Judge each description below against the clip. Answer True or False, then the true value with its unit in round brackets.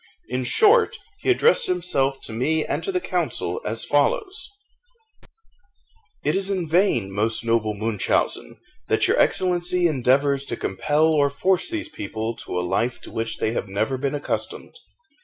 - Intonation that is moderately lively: False (8.9 semitones)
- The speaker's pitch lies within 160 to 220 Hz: False (140 Hz)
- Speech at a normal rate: True (160 wpm)